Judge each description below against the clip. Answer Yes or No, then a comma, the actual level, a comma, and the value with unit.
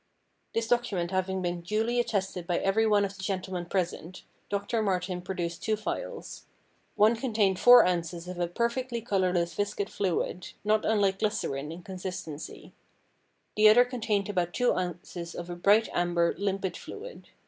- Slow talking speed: No, average, 155 wpm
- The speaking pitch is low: No, high, 190 Hz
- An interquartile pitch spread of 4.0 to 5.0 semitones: No, average, 3.5 semitones